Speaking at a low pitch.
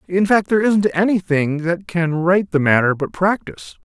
No: medium, 170 Hz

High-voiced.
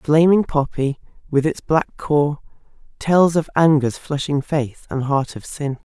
No: medium, 145 Hz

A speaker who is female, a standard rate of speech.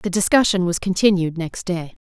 Yes: female; average, 175 wpm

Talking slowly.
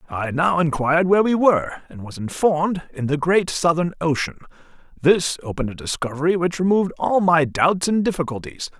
No: average, 170 wpm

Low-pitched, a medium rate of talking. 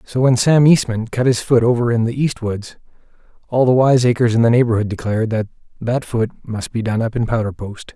No: low, 120 Hz; fast, 220 wpm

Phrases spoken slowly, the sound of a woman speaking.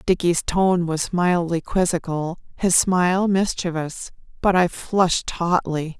Yes: slow, 120 wpm; female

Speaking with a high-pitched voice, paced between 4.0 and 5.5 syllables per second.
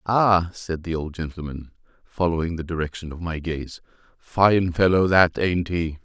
No: very low, 85 Hz; 4.5 syllables/s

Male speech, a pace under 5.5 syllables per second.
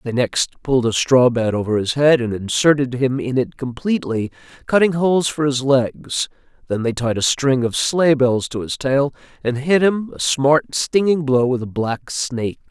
Yes: male; 4.7 syllables/s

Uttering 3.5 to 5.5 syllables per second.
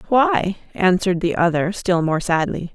Yes: 4.7 syllables/s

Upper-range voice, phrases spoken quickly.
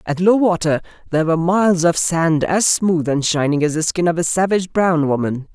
No: medium, 170 Hz; fast, 215 wpm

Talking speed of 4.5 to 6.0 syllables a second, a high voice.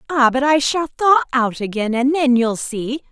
Yes: 4.7 syllables/s; very high, 260 Hz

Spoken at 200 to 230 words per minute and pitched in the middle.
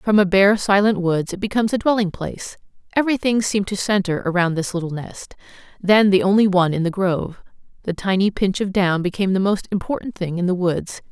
No: fast, 205 wpm; high, 195 Hz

